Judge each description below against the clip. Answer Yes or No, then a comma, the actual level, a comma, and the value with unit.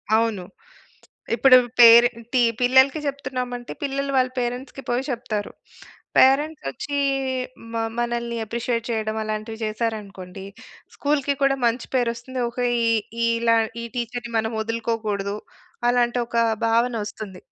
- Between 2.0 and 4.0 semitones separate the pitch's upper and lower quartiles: Yes, narrow, 2.4 semitones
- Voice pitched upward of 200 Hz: Yes, high, 235 Hz